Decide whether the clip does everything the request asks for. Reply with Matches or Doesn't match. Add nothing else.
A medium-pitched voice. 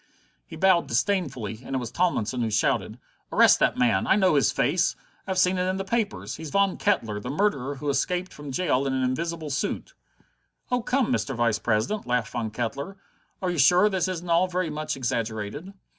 Matches